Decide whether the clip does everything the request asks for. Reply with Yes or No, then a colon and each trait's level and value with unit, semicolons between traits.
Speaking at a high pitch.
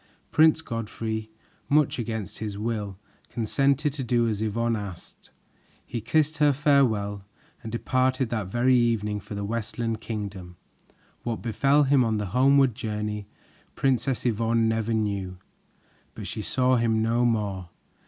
No: low, 115 Hz